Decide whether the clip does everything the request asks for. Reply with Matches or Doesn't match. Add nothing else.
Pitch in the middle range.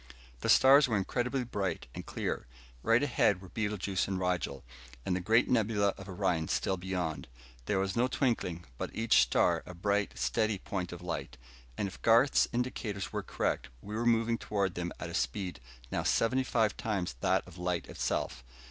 Doesn't match